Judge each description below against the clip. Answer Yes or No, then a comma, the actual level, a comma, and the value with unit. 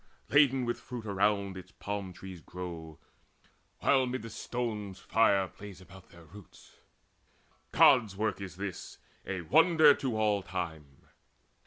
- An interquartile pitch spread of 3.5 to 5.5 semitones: Yes, average, 4.3 semitones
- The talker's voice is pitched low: Yes, low, 100 Hz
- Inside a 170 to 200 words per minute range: No, slow, 135 wpm